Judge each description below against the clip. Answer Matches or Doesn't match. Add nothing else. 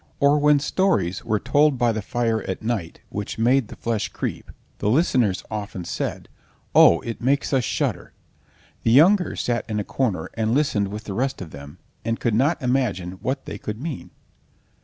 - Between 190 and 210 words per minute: Doesn't match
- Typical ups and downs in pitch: Matches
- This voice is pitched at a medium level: Doesn't match